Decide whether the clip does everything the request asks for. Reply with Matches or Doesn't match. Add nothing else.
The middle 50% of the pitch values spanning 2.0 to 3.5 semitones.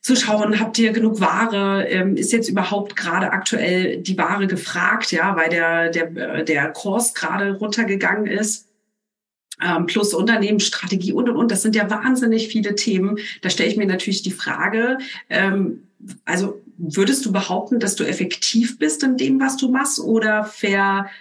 Matches